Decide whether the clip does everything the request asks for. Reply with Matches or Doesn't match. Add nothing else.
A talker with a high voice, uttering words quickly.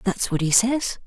Matches